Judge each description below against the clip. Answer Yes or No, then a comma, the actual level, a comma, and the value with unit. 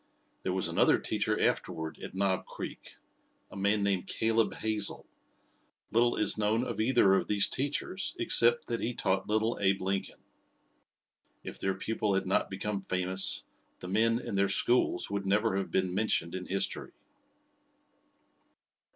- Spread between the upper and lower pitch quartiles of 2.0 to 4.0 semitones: Yes, average, 2.7 semitones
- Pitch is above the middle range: No, low, 100 Hz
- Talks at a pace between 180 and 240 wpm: No, average, 150 wpm